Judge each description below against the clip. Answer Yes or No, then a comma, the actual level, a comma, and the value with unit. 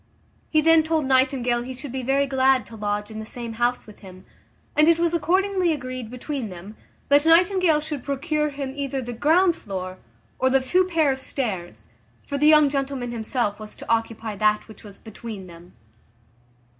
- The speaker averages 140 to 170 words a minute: No, average, 185 wpm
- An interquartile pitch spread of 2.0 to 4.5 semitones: No, wide, 5.5 semitones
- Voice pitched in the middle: No, very high, 260 Hz